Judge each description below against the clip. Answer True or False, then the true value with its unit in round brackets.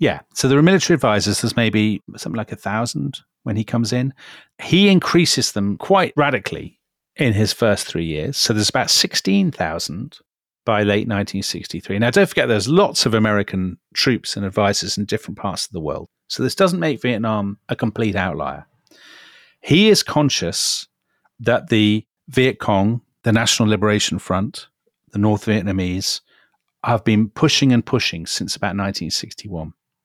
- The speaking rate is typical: True (170 wpm)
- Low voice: True (110 Hz)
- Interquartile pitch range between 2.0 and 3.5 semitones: False (4.3 semitones)